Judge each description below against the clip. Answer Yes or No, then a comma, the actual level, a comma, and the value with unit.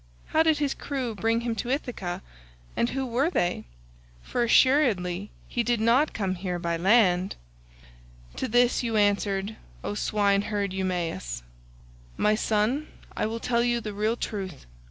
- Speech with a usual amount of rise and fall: Yes, average, 4.5 semitones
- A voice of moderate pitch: No, high, 215 Hz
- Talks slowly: No, average, 145 wpm